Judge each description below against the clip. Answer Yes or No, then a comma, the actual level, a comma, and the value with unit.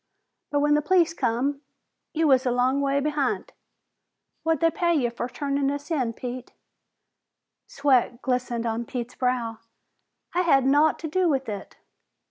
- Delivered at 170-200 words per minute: No, average, 155 wpm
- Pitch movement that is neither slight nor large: Yes, average, 3.3 semitones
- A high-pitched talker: Yes, very high, 275 Hz